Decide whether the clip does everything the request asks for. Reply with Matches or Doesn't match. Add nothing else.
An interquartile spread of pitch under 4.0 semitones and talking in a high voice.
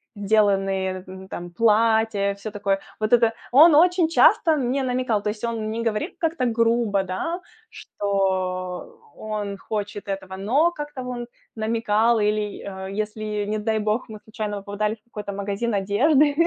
Matches